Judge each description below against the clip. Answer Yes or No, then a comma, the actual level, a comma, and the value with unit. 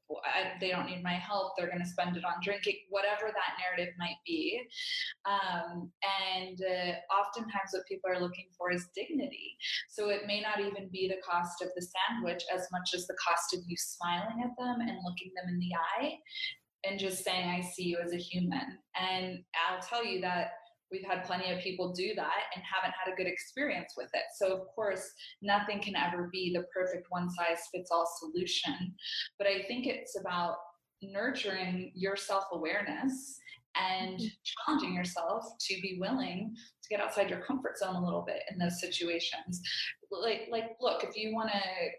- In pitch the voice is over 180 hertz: Yes, high, 190 Hz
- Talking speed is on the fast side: No, average, 185 wpm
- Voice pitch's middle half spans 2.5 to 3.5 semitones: Yes, average, 2.9 semitones